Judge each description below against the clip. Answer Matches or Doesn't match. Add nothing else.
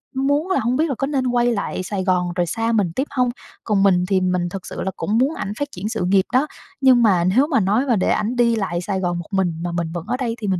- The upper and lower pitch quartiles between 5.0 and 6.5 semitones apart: Matches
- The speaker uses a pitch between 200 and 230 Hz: Matches